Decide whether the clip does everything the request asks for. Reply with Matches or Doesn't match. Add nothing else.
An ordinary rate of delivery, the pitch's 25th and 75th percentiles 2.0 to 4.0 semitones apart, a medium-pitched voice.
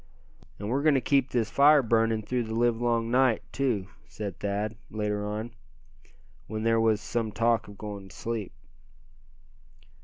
Doesn't match